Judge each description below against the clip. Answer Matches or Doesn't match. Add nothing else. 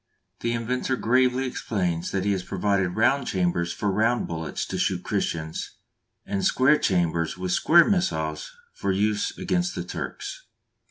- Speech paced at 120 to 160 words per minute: Matches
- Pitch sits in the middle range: Doesn't match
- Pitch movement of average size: Doesn't match